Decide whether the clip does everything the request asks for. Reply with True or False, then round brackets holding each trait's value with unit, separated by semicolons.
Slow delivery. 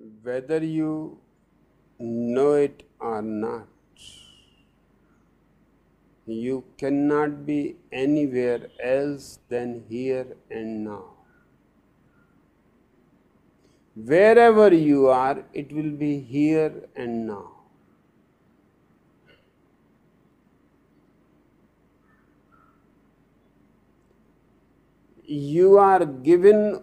True (60 wpm)